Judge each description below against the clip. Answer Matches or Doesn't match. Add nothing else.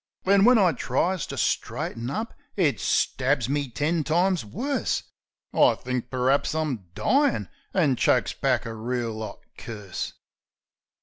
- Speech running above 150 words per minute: Doesn't match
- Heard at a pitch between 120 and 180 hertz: Matches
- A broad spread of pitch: Matches